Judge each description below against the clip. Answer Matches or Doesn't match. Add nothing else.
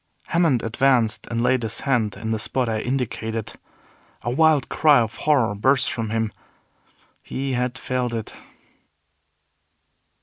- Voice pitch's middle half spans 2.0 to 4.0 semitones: Matches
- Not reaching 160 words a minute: Matches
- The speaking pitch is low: Matches